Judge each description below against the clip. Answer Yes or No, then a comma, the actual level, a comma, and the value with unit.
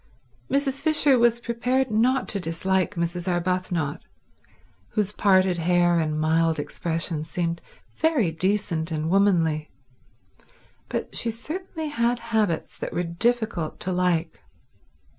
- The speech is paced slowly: Yes, slow, 120 wpm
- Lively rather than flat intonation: Yes, wide, 6.0 semitones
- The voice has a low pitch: No, medium, 185 Hz